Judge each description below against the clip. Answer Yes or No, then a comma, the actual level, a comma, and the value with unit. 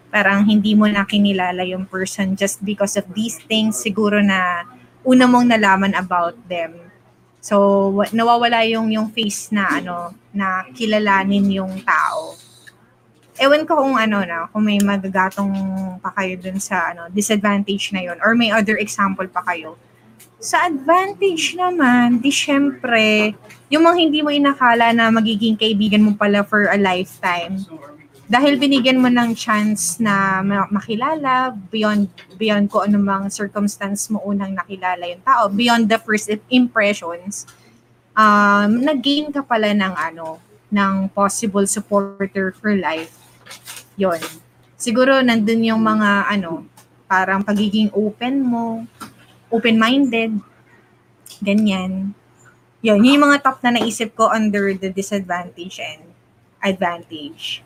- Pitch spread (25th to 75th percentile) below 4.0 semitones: Yes, average, 2.9 semitones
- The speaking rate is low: Yes, slow, 130 wpm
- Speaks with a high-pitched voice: Yes, high, 210 Hz